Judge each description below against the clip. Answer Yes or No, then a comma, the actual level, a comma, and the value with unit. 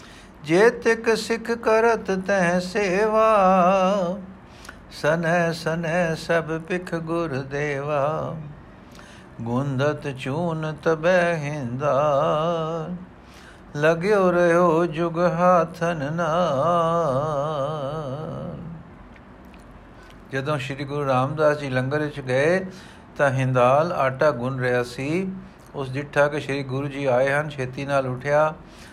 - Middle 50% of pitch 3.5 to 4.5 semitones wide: Yes, average, 4.0 semitones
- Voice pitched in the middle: Yes, medium, 155 Hz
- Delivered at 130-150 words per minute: No, slow, 95 wpm